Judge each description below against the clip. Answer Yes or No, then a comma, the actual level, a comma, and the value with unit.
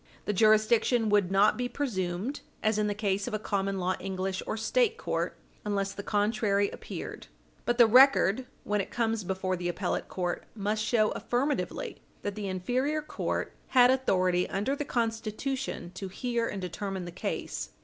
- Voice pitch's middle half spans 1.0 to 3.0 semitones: No, average, 3.9 semitones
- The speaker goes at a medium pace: Yes, average, 170 wpm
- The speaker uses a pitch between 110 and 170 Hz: No, high, 210 Hz